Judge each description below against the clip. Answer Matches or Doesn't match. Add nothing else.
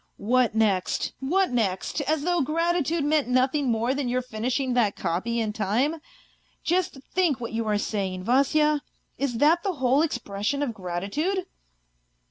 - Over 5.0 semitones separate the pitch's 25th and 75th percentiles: Matches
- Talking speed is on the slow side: Doesn't match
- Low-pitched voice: Doesn't match